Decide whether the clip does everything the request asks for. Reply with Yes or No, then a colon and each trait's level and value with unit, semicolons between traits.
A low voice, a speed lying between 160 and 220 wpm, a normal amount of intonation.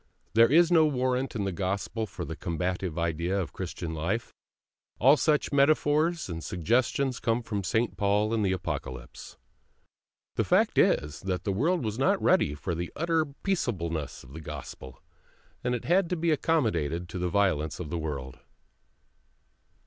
No: low, 100 Hz; average, 165 wpm; wide, 8.6 semitones